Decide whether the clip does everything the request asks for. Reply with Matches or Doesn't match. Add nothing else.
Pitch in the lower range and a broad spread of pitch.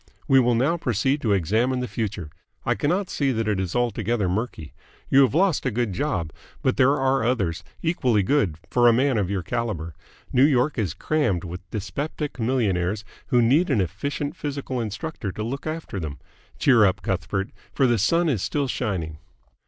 Matches